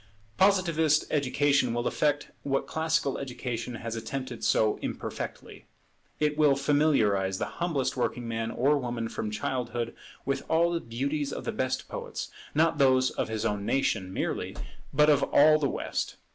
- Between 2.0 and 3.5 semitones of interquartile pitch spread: No, average, 4.4 semitones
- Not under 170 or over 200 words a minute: No, average, 155 wpm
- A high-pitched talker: No, low, 135 Hz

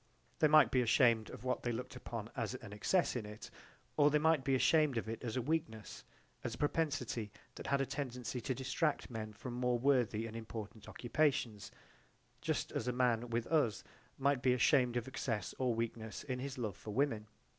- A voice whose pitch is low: Yes, low, 125 Hz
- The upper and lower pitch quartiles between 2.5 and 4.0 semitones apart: Yes, average, 3.3 semitones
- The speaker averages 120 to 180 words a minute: No, average, 200 wpm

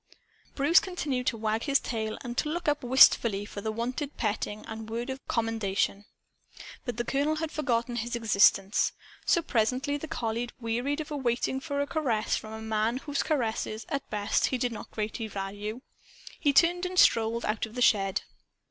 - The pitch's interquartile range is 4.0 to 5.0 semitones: Yes, average, 4.3 semitones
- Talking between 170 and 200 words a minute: Yes, average, 180 wpm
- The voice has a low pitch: No, high, 235 Hz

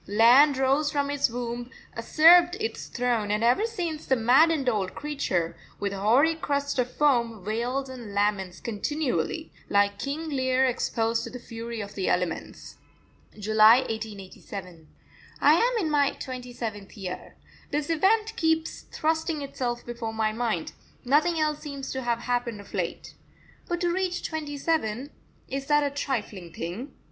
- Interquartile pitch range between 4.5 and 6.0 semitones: Yes, wide, 5.4 semitones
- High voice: Yes, very high, 250 Hz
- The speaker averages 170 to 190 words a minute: No, average, 155 wpm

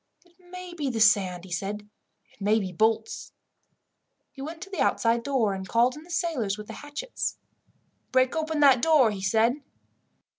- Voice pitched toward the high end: Yes, very high, 250 Hz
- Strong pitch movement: Yes, wide, 7.0 semitones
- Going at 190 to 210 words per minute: No, average, 180 wpm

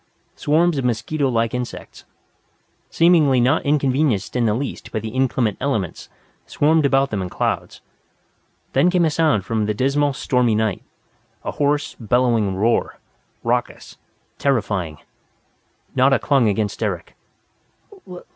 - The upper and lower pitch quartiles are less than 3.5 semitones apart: No, average, 4.7 semitones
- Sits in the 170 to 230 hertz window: No, low, 125 Hz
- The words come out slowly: Yes, slow, 130 wpm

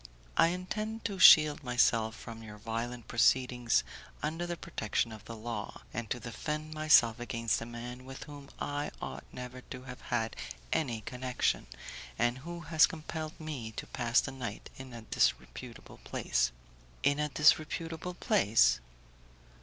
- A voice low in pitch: Yes, low, 125 Hz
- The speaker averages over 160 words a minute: No, average, 150 wpm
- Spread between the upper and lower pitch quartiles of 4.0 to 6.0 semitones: Yes, average, 4.9 semitones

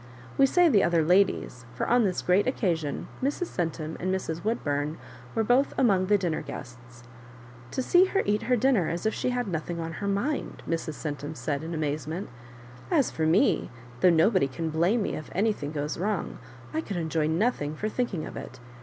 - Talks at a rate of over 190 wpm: Yes, average, 200 wpm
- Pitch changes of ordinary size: No, wide, 5.9 semitones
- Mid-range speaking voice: Yes, medium, 175 Hz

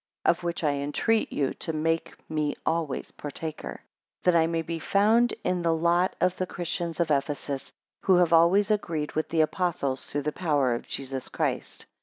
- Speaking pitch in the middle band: Yes, medium, 165 Hz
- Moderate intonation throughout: Yes, average, 3.0 semitones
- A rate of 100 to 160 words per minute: No, average, 185 wpm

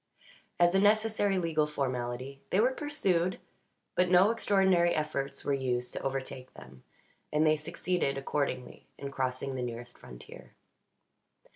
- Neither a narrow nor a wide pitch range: No, wide, 5.8 semitones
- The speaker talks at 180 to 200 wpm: No, slow, 135 wpm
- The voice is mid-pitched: Yes, medium, 150 Hz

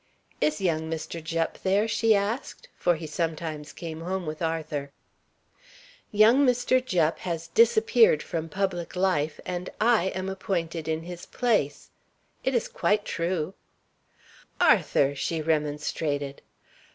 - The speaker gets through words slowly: Yes, slow, 125 wpm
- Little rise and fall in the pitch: No, average, 4.1 semitones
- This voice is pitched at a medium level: Yes, medium, 170 Hz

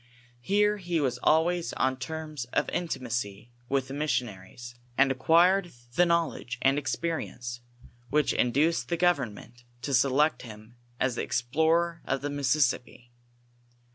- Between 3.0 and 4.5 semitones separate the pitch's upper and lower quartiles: No, average, 5.2 semitones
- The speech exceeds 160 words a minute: No, slow, 135 wpm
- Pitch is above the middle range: No, medium, 140 Hz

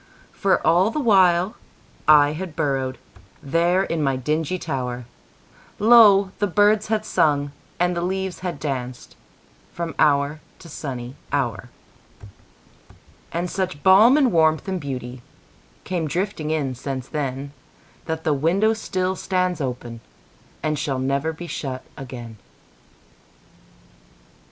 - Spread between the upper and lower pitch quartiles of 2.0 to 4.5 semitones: No, wide, 5.6 semitones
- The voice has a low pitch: No, medium, 155 Hz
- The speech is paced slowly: Yes, slow, 110 wpm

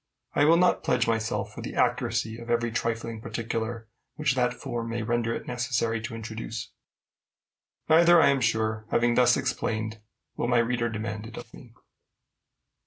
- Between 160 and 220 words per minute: Yes, average, 165 wpm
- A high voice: No, low, 115 Hz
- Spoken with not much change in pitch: Yes, narrow, 1.6 semitones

